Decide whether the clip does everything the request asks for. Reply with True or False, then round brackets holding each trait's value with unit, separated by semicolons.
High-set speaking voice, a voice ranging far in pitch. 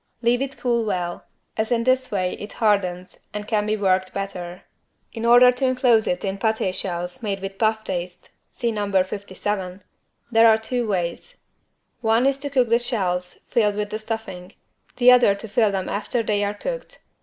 False (210 Hz; 3.7 semitones)